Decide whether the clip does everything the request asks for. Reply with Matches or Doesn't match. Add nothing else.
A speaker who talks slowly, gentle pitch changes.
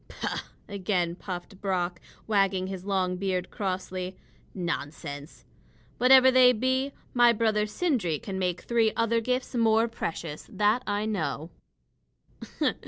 Doesn't match